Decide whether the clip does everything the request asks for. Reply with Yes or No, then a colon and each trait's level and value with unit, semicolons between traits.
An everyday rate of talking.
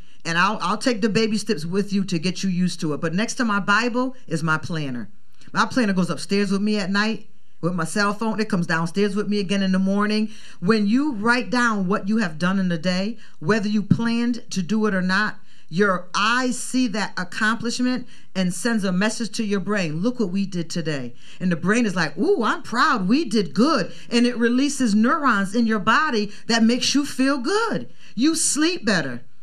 No: fast, 215 wpm